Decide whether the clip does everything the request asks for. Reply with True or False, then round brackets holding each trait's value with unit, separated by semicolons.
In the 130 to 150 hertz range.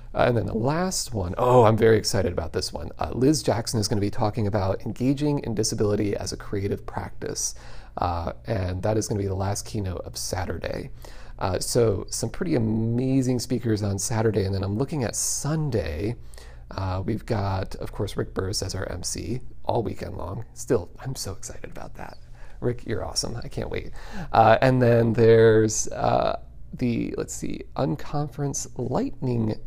False (110 Hz)